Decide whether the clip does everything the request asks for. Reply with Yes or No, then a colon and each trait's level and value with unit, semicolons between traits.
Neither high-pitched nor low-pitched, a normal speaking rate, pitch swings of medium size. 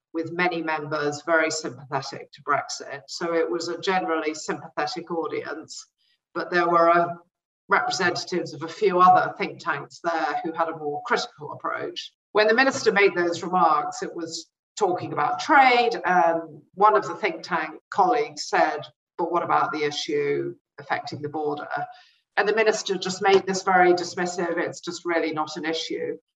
Yes: medium, 175 Hz; average, 165 wpm; average, 4.7 semitones